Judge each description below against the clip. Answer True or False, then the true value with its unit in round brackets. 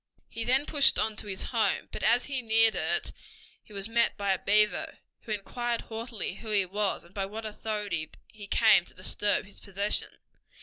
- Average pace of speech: True (190 wpm)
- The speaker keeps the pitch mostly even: True (2.3 semitones)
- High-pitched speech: True (210 Hz)